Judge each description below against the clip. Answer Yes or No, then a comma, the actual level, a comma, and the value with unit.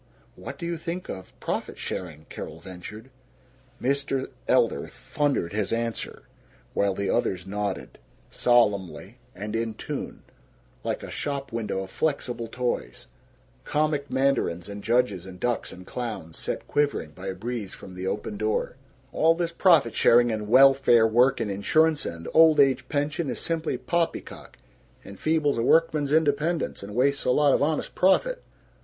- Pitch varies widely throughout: Yes, wide, 6.5 semitones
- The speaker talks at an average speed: Yes, average, 150 wpm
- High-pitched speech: No, low, 120 Hz